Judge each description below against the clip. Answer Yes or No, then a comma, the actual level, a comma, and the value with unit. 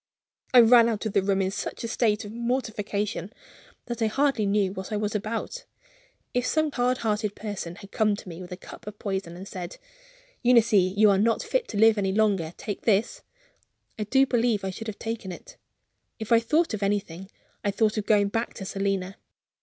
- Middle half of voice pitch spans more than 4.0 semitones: No, average, 2.8 semitones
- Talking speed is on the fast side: Yes, fast, 210 wpm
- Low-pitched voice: No, high, 210 Hz